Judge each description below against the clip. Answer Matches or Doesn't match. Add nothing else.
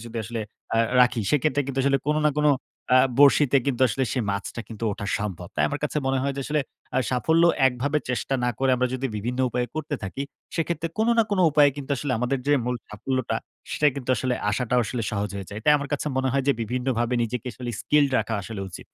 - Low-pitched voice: Matches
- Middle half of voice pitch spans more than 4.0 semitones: Doesn't match